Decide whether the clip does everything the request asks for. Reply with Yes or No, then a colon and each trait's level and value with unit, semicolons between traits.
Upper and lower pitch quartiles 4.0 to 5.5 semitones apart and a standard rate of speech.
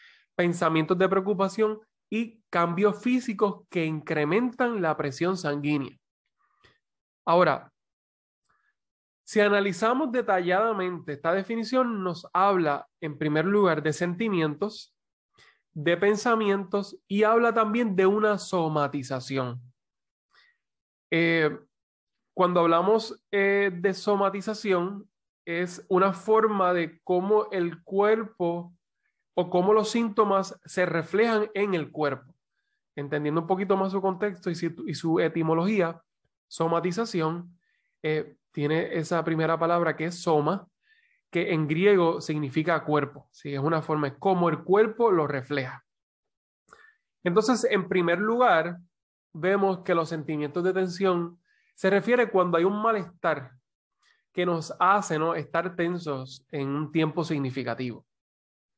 No: average, 4.3 semitones; slow, 115 wpm